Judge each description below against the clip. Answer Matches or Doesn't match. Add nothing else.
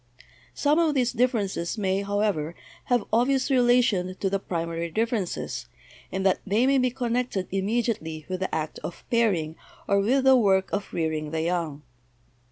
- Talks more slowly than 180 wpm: Matches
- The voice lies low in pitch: Doesn't match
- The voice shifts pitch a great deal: Matches